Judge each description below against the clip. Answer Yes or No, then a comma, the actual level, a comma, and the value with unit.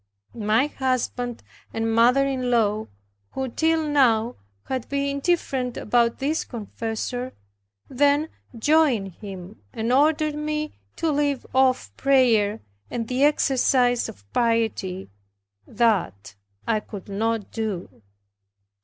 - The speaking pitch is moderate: No, high, 245 Hz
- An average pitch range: Yes, average, 4.0 semitones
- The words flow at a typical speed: No, slow, 110 wpm